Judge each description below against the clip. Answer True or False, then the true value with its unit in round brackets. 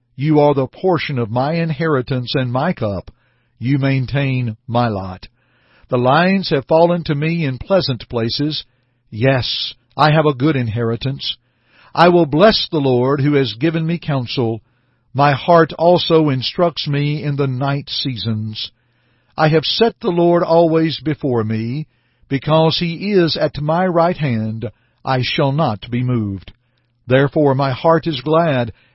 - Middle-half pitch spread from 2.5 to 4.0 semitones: False (4.7 semitones)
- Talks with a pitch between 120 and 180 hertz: True (140 Hz)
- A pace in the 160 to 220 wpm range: False (150 wpm)